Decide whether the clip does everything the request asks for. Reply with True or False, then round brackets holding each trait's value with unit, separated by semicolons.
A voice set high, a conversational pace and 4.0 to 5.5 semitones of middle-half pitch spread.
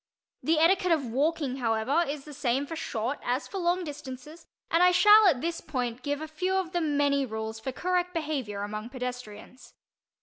True (285 Hz; 190 wpm; 5.1 semitones)